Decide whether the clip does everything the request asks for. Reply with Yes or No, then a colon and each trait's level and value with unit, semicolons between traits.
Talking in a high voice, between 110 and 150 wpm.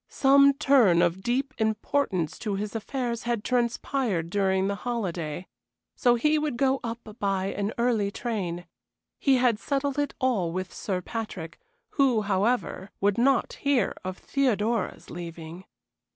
Yes: high, 220 Hz; average, 140 wpm